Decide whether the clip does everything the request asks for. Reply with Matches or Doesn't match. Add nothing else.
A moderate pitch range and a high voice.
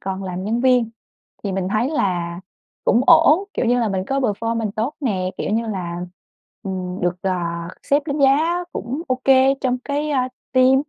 Doesn't match